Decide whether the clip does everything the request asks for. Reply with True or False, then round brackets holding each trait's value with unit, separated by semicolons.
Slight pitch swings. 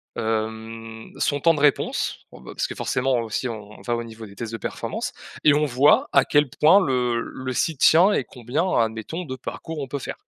False (4.5 semitones)